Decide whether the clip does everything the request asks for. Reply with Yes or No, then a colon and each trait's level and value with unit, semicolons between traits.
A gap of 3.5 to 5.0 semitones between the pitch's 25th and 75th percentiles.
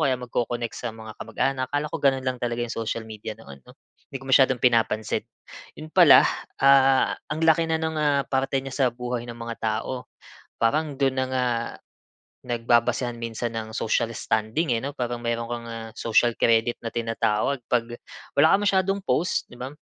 No: average, 2.8 semitones